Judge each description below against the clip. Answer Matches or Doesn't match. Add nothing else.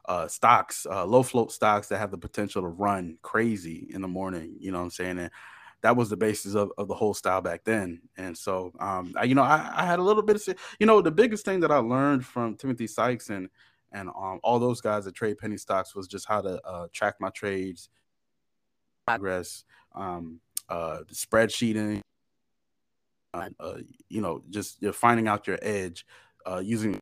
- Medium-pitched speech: Doesn't match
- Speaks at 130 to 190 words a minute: Doesn't match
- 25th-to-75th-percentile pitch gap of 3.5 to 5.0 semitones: Matches